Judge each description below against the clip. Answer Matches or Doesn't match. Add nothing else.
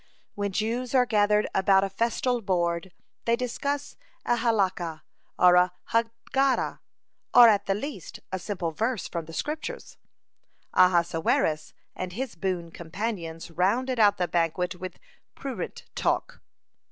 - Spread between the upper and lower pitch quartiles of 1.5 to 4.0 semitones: Doesn't match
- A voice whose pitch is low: Doesn't match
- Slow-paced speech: Matches